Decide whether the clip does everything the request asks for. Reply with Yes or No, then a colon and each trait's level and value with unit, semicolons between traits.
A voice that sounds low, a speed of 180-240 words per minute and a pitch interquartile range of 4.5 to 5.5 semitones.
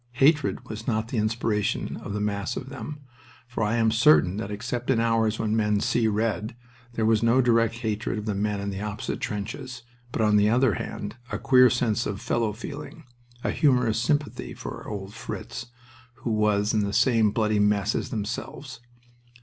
No: low, 110 Hz; average, 185 wpm; narrow, 2.5 semitones